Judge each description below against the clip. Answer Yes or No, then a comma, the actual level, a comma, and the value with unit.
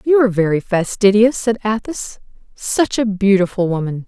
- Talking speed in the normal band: Yes, average, 145 wpm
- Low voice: No, high, 210 Hz